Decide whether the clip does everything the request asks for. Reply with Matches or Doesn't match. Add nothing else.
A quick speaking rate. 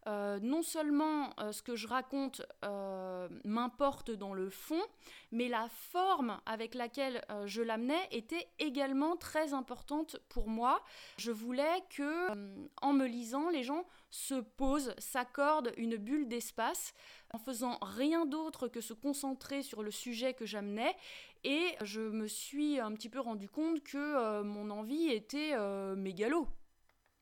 Doesn't match